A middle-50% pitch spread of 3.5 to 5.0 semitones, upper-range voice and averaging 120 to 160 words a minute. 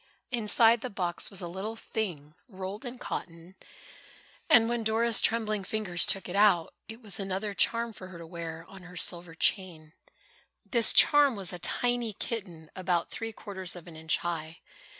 No: average, 4.5 semitones; high, 195 Hz; average, 170 wpm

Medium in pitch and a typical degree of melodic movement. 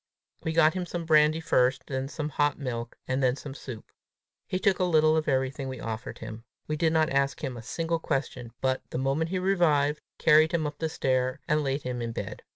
Yes: medium, 145 Hz; average, 3.5 semitones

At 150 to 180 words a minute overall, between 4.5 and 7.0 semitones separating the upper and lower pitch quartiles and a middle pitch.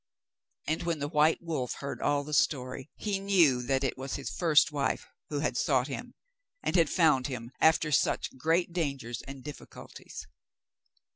No: average, 165 wpm; average, 3.5 semitones; medium, 145 Hz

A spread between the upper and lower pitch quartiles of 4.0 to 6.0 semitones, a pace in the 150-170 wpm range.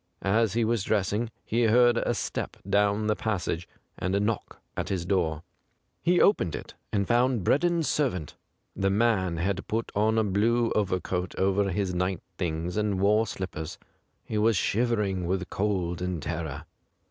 No: average, 3.5 semitones; average, 165 wpm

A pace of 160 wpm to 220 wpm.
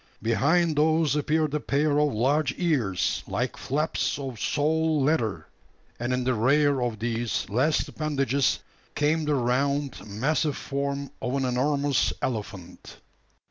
No: slow, 135 wpm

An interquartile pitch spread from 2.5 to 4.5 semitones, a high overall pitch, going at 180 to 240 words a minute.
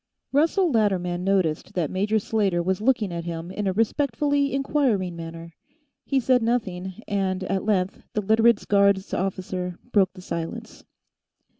No: average, 3.9 semitones; high, 195 Hz; average, 145 wpm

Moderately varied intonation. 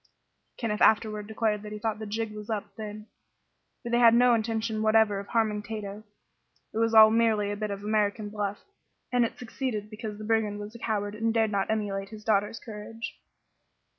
No: narrow, 1.3 semitones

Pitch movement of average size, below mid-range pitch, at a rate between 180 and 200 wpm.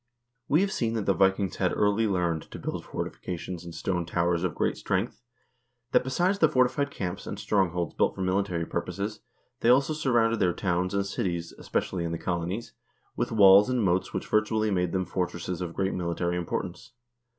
Yes: average, 4.3 semitones; very low, 95 Hz; average, 195 wpm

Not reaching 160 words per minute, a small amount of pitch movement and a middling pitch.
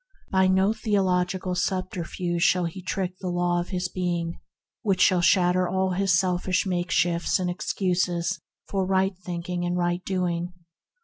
Yes: average, 145 wpm; narrow, 1.2 semitones; medium, 180 Hz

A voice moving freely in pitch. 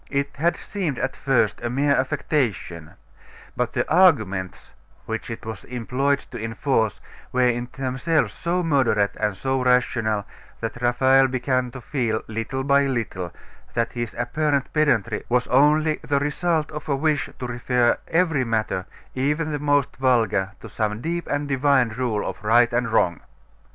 No: average, 4.0 semitones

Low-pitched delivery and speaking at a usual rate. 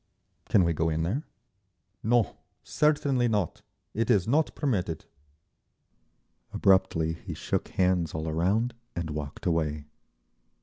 No: very low, 90 Hz; slow, 120 wpm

